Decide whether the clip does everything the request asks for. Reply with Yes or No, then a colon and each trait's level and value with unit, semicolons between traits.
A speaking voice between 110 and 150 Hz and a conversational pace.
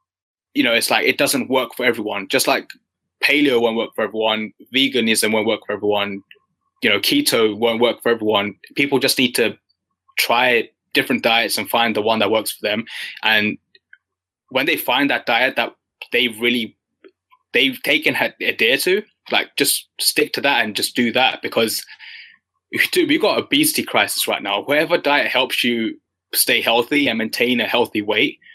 Yes: medium, 140 Hz; average, 180 wpm